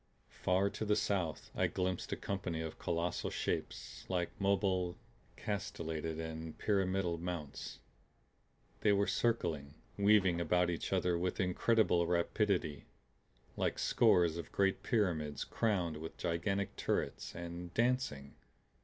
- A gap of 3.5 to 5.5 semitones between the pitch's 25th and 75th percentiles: No, average, 3.1 semitones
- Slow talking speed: Yes, slow, 120 wpm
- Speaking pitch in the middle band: No, very low, 90 Hz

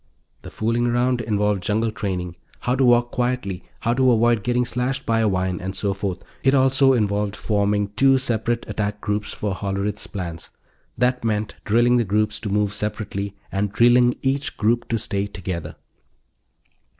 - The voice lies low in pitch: Yes, low, 110 Hz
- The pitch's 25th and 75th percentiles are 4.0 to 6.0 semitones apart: No, average, 3.2 semitones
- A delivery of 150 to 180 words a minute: Yes, average, 165 wpm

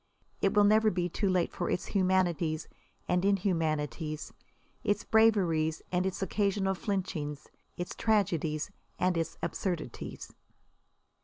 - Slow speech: Yes, slow, 120 wpm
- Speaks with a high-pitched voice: No, medium, 180 Hz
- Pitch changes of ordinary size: Yes, average, 3.7 semitones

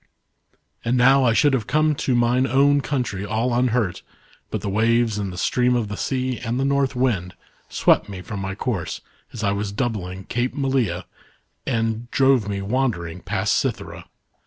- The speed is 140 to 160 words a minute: No, average, 180 wpm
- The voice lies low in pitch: Yes, low, 120 Hz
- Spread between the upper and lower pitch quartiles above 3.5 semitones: Yes, average, 4.2 semitones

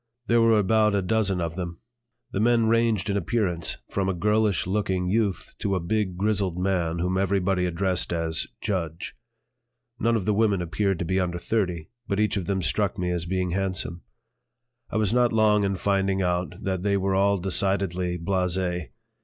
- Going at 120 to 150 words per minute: No, average, 180 wpm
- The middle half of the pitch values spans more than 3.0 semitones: No, average, 2.7 semitones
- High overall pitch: No, very low, 95 Hz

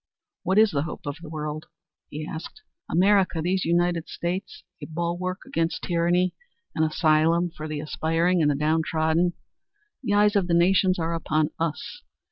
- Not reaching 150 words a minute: No, average, 160 wpm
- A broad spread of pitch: No, narrow, 2.5 semitones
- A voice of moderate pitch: Yes, medium, 170 Hz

